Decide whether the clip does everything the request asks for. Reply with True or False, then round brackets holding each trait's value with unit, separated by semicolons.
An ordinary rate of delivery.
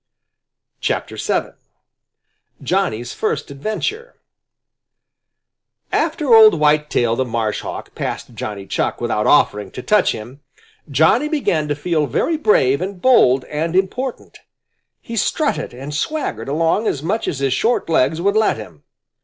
False (130 wpm)